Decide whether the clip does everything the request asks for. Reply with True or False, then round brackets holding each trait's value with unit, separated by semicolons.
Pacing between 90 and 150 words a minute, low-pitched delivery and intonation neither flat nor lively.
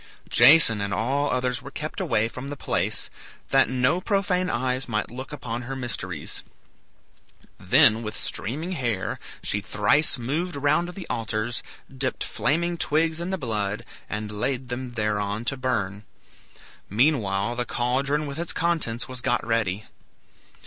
True (145 wpm; 125 Hz; 4.9 semitones)